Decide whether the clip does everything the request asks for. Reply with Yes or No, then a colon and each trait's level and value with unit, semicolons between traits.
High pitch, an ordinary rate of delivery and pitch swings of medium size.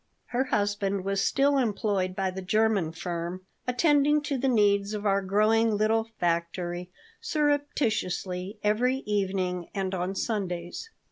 No: high, 205 Hz; slow, 130 wpm; average, 3.8 semitones